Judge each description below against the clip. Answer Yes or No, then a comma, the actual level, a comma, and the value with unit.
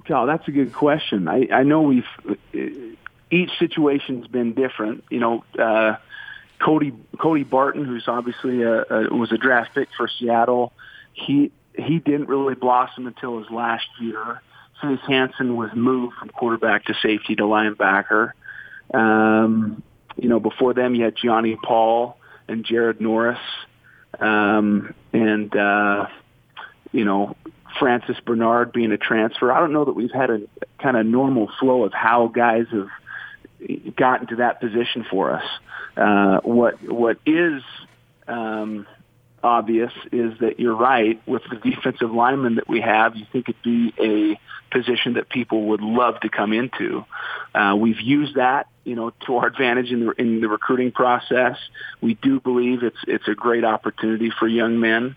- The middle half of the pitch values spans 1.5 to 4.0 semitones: Yes, narrow, 2.4 semitones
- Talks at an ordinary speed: Yes, average, 160 wpm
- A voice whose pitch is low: Yes, low, 120 Hz